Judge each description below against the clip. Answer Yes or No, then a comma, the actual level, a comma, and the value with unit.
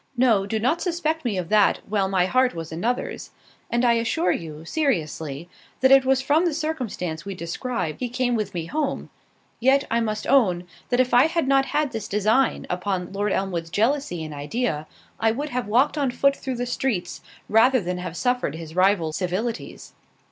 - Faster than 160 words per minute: Yes, average, 185 wpm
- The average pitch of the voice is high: Yes, high, 225 Hz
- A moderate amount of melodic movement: No, wide, 6.5 semitones